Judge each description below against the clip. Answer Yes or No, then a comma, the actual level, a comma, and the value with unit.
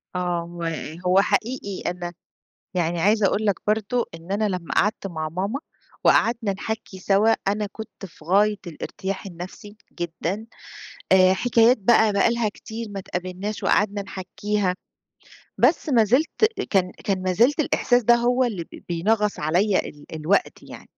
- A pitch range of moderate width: Yes, average, 3.4 semitones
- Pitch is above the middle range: Yes, high, 200 Hz